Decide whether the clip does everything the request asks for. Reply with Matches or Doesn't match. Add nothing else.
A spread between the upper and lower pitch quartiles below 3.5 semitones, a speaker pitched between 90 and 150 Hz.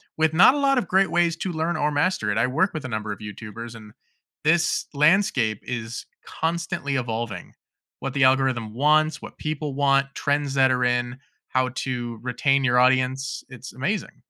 Doesn't match